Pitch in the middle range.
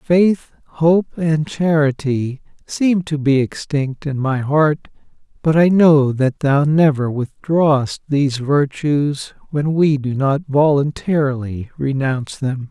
Yes: medium, 145 Hz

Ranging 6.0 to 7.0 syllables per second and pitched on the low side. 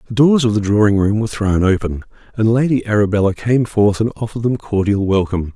Yes: 6.2 syllables/s; low, 105 Hz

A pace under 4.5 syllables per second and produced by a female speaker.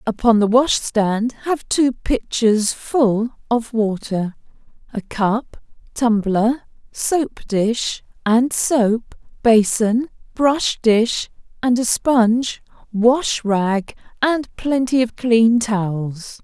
Yes: 2.8 syllables/s; female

